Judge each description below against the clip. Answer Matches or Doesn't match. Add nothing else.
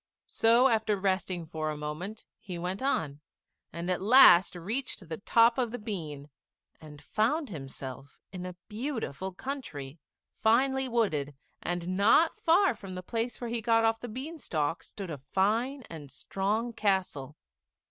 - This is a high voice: Matches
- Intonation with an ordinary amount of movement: Doesn't match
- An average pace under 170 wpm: Matches